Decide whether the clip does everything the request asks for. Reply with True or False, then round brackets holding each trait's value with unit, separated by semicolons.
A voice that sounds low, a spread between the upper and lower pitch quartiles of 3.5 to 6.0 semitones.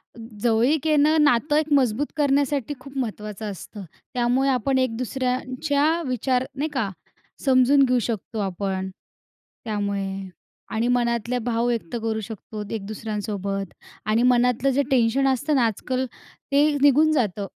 False (245 Hz; 4.0 semitones)